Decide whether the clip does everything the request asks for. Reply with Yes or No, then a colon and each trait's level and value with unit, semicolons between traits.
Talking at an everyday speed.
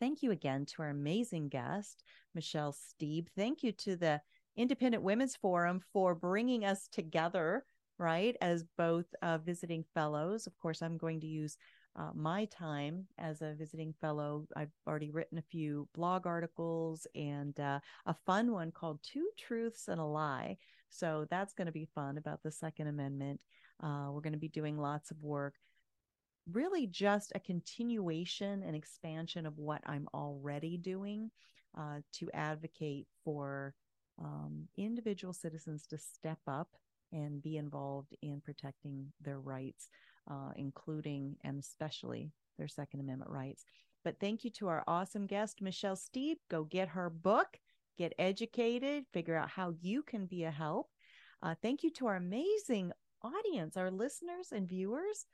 Yes: average, 160 wpm